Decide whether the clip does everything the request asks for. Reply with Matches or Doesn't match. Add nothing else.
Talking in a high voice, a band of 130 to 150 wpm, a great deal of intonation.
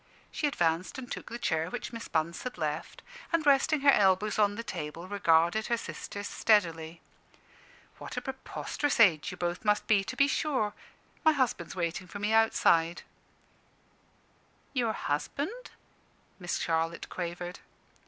Matches